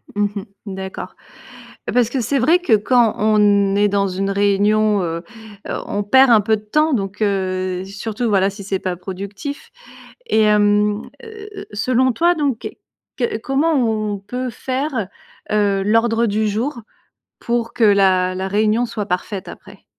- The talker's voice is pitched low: No, high, 210 Hz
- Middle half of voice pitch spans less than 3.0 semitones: No, average, 3.3 semitones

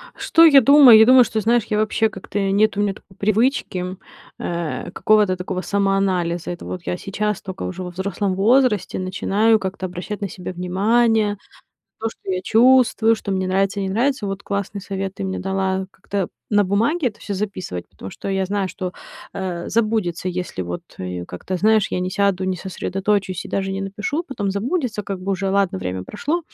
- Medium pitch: No, high, 195 Hz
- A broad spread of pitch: No, narrow, 2.6 semitones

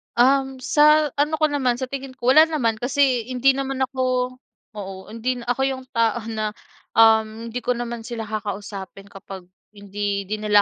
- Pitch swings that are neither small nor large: Yes, average, 3.7 semitones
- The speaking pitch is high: Yes, high, 240 Hz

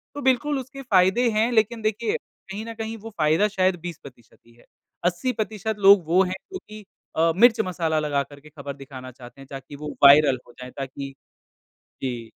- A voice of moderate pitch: Yes, medium, 180 Hz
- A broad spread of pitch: Yes, wide, 7.8 semitones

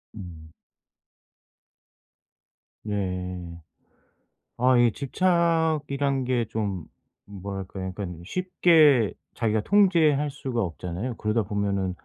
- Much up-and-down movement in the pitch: Yes, wide, 7.0 semitones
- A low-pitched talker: Yes, low, 110 Hz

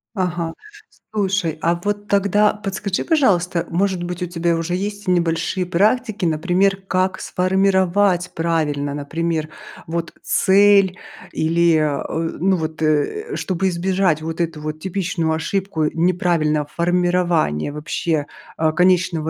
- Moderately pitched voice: Yes, medium, 175 Hz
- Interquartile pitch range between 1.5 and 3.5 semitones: Yes, average, 2.9 semitones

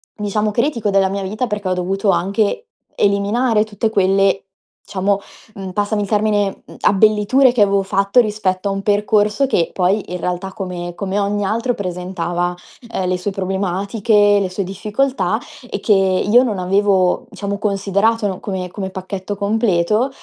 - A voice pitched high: Yes, high, 200 Hz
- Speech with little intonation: Yes, narrow, 1.9 semitones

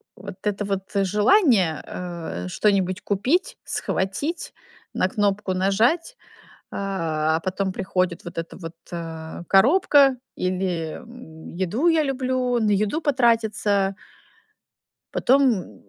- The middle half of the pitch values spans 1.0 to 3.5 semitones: No, average, 5.3 semitones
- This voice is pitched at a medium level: No, high, 195 Hz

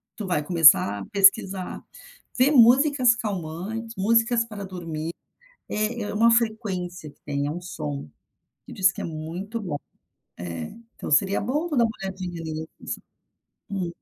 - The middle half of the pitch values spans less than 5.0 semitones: No, wide, 5.6 semitones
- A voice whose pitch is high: Yes, high, 195 Hz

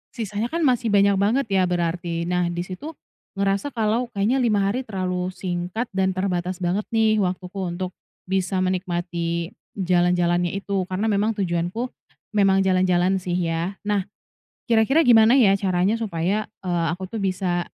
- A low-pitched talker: No, high, 190 Hz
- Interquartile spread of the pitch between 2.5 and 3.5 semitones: Yes, average, 2.9 semitones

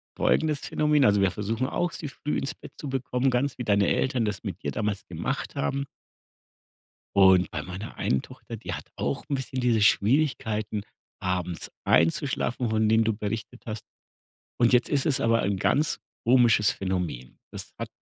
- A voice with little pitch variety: No, average, 4.6 semitones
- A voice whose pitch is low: Yes, low, 110 Hz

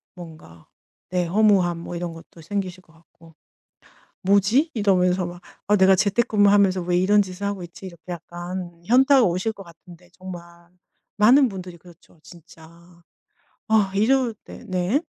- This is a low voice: No, medium, 185 Hz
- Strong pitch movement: No, average, 2.9 semitones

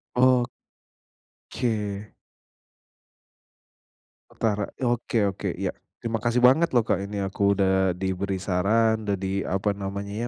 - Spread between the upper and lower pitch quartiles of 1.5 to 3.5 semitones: Yes, average, 2.8 semitones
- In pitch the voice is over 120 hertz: No, low, 100 Hz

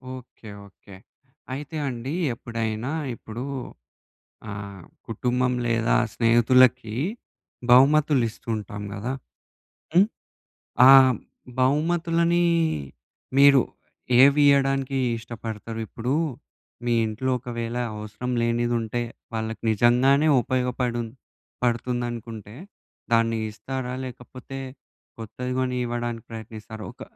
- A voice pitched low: Yes, low, 120 Hz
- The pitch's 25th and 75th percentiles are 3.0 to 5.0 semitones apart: No, narrow, 2.5 semitones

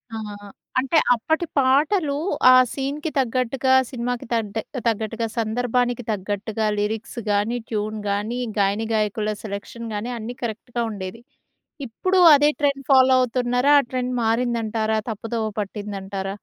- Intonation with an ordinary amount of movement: Yes, average, 3.1 semitones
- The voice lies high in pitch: Yes, high, 230 Hz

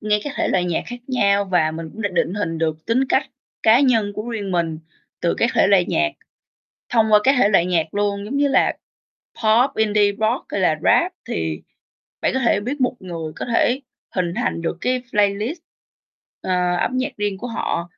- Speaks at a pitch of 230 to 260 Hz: No, high, 205 Hz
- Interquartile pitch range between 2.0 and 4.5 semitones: No, average, 5.1 semitones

